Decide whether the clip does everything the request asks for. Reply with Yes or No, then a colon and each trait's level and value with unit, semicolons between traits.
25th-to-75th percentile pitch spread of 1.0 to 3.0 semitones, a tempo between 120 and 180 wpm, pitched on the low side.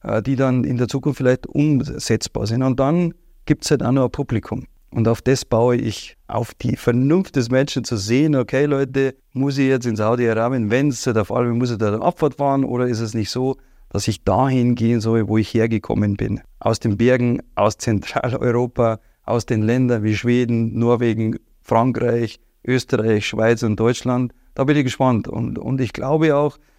No: average, 2.7 semitones; fast, 190 wpm; low, 125 Hz